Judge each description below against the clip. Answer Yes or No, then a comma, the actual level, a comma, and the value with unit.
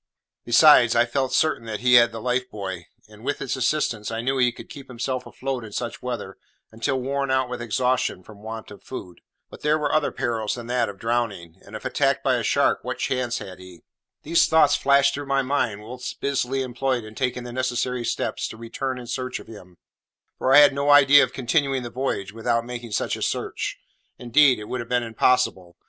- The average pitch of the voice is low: Yes, low, 125 Hz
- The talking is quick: Yes, fast, 215 wpm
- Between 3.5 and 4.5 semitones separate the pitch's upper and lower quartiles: No, average, 2.9 semitones